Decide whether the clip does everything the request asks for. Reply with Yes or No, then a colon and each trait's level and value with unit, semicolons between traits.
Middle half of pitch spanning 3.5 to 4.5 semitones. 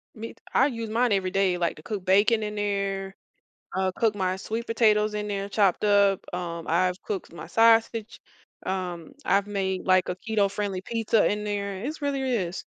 No: narrow, 2.6 semitones